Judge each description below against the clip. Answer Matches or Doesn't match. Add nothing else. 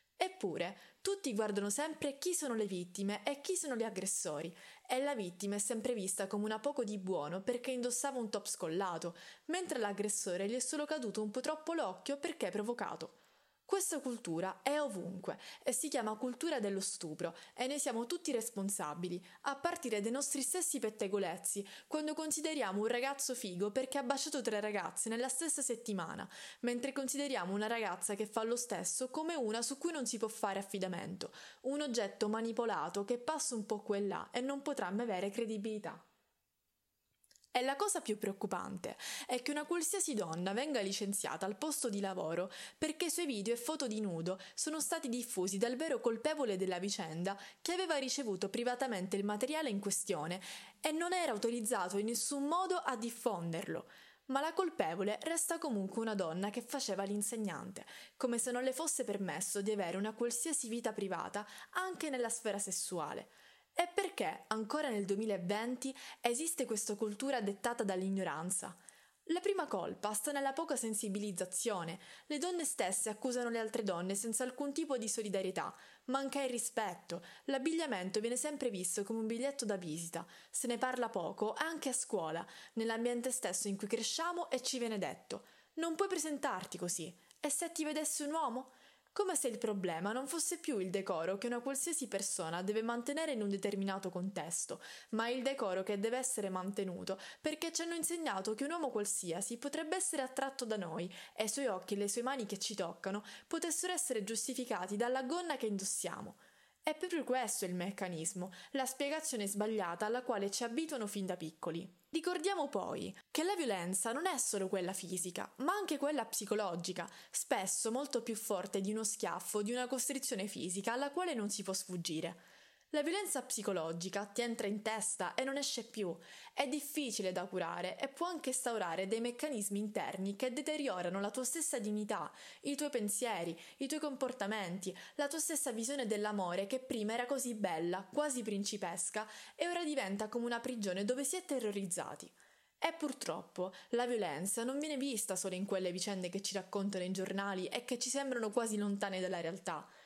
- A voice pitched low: Doesn't match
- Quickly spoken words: Matches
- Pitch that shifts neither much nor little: Doesn't match